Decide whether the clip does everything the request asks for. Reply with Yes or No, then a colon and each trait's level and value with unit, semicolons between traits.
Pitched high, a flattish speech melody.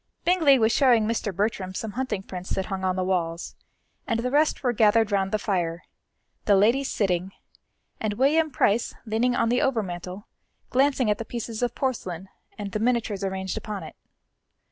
No: high, 215 Hz; average, 4.2 semitones